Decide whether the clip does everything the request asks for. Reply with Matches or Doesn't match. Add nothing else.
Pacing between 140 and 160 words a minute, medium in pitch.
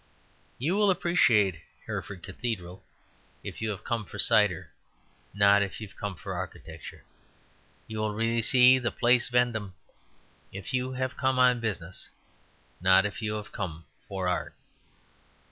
Doesn't match